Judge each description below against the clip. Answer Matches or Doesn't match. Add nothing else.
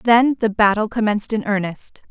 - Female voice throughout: Matches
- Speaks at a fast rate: Doesn't match